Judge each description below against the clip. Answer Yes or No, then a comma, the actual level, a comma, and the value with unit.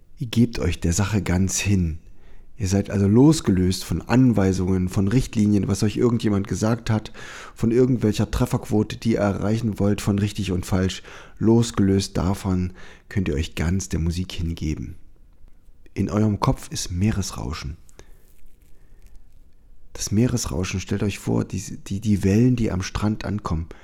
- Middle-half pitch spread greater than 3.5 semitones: No, average, 3.0 semitones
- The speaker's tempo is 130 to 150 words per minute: Yes, average, 145 wpm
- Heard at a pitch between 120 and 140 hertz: No, low, 100 Hz